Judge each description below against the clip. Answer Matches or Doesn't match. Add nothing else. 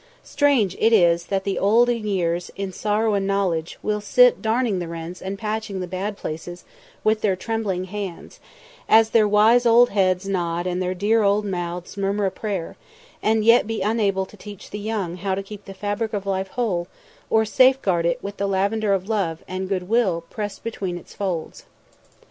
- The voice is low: Doesn't match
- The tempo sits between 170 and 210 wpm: Matches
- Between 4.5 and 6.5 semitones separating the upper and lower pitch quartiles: Doesn't match